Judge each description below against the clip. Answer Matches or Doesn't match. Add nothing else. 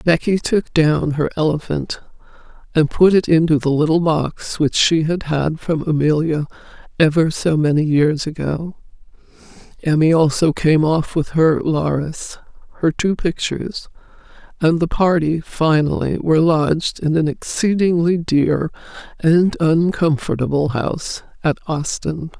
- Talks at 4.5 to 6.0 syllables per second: Doesn't match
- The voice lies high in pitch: Doesn't match